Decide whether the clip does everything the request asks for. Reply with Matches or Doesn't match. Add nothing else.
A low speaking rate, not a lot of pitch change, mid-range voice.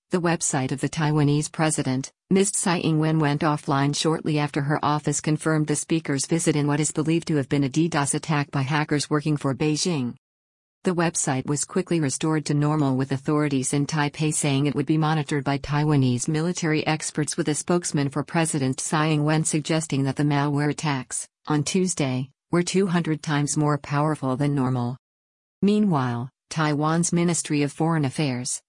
Doesn't match